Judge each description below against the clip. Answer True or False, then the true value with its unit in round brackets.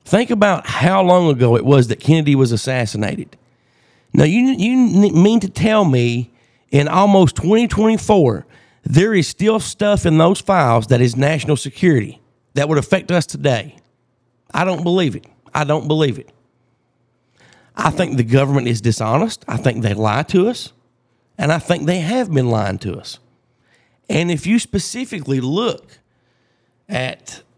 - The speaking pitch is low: False (150 Hz)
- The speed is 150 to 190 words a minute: True (155 wpm)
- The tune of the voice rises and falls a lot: True (7.4 semitones)